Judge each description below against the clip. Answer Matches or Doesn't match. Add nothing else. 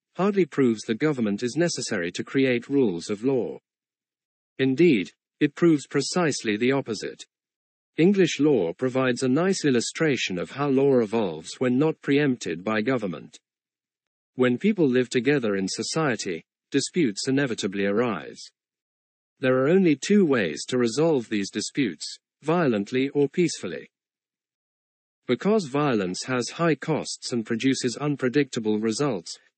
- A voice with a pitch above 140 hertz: Doesn't match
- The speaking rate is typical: Doesn't match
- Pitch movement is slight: Doesn't match